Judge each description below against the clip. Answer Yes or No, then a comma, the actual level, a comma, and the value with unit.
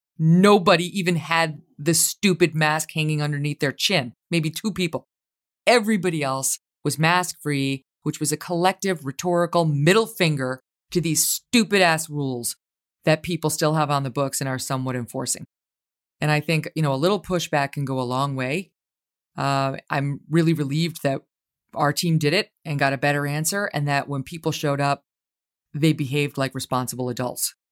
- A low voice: No, medium, 150 Hz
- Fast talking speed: No, average, 165 wpm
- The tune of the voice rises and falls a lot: No, average, 4.0 semitones